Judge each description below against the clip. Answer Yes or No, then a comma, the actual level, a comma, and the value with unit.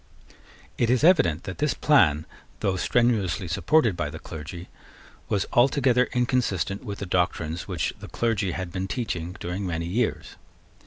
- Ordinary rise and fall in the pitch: No, wide, 5.8 semitones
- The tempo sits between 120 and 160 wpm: Yes, average, 150 wpm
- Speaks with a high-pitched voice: No, very low, 95 Hz